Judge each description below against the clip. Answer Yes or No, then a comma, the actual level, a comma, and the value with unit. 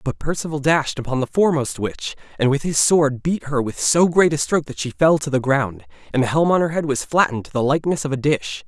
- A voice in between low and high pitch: Yes, medium, 145 Hz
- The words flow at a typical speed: No, fast, 265 wpm